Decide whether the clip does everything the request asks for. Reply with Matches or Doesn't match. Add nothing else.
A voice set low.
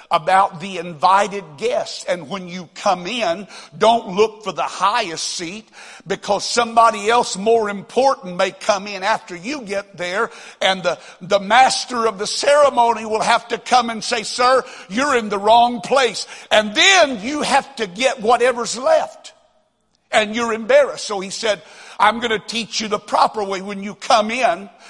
Doesn't match